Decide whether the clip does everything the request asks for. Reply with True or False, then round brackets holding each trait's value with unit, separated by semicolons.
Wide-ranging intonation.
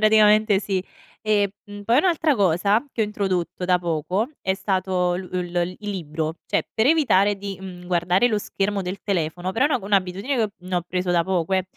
False (2.7 semitones)